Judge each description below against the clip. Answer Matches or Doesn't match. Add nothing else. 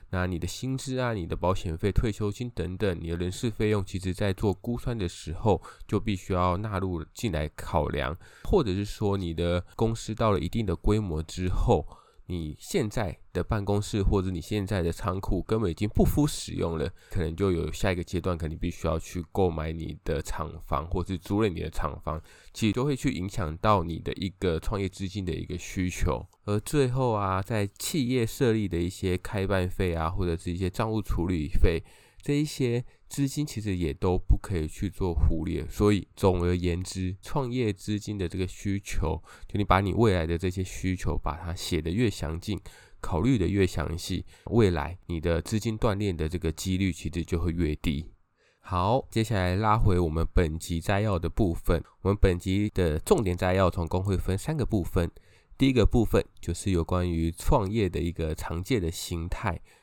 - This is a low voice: Matches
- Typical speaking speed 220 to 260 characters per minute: Doesn't match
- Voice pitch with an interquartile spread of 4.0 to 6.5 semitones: Doesn't match